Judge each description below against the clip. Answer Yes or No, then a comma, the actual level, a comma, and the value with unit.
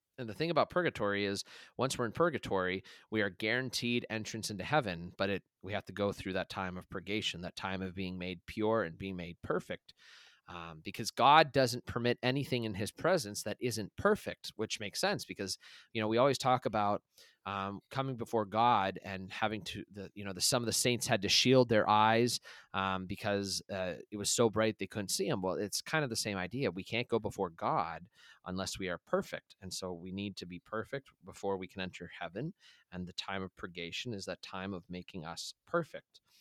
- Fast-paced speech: Yes, fast, 215 wpm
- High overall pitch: No, low, 100 Hz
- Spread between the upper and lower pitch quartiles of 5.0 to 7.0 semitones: No, average, 3.6 semitones